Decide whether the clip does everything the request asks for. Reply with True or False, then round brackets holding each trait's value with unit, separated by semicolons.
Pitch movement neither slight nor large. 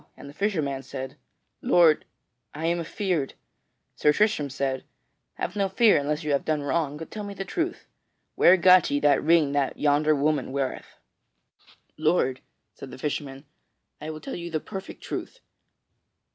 True (4.2 semitones)